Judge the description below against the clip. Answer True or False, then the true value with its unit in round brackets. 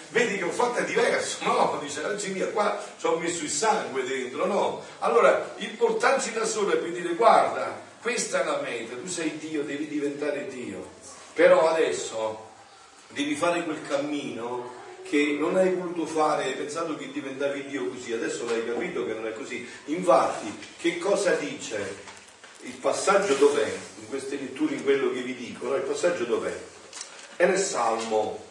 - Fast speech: True (175 wpm)